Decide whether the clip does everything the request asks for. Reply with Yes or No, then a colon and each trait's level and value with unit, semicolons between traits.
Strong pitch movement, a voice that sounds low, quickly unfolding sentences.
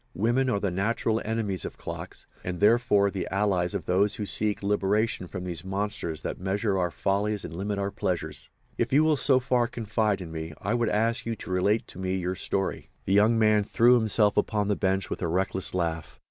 No: average, 2.9 semitones; low, 100 Hz; fast, 215 wpm